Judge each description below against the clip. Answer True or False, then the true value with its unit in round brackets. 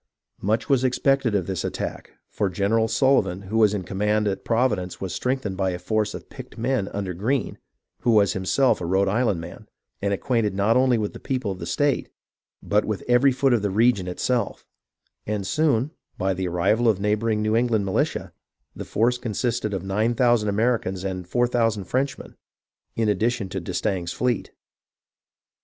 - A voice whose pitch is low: True (105 Hz)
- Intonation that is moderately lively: True (3.9 semitones)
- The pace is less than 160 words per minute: False (185 wpm)